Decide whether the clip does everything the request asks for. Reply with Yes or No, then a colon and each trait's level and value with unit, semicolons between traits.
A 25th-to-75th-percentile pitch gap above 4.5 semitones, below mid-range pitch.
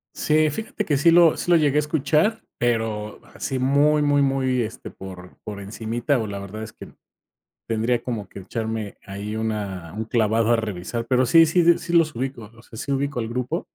Yes: average, 5.0 semitones; low, 120 Hz